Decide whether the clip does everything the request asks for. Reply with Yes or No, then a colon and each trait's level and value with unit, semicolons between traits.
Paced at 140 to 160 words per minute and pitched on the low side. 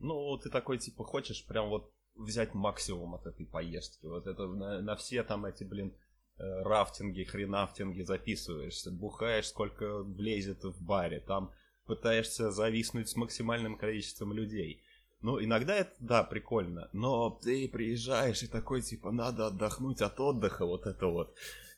Yes: average, 145 wpm; low, 110 Hz